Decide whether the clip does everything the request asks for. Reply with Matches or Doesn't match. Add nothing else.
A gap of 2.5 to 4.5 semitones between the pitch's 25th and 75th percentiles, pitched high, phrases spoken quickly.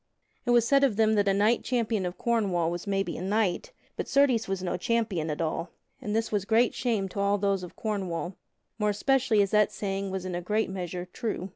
Matches